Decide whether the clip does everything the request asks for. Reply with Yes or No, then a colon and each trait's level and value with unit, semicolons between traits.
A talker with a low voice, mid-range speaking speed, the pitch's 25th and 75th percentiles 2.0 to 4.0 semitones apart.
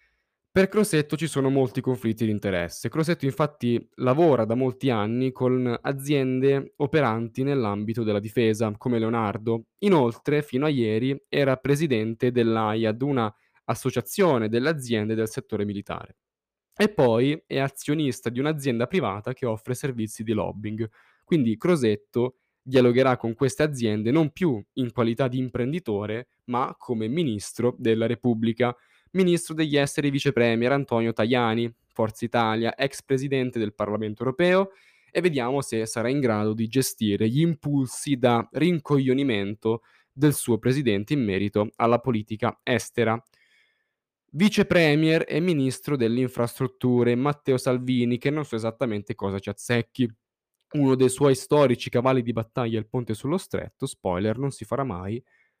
Yes: low, 125 Hz; average, 140 wpm; average, 3.7 semitones